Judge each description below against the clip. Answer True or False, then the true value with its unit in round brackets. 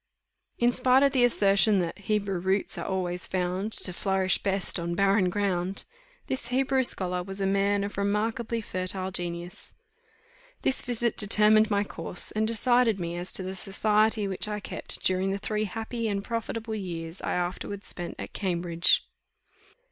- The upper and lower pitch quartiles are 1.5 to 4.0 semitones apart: True (3.0 semitones)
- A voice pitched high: True (200 Hz)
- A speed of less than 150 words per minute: False (170 wpm)